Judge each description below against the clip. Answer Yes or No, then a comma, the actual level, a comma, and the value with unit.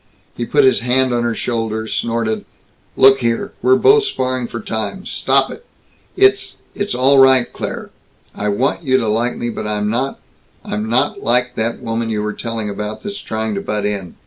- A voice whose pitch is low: Yes, low, 120 Hz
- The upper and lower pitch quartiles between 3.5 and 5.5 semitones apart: No, average, 3.0 semitones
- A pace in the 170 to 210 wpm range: Yes, average, 190 wpm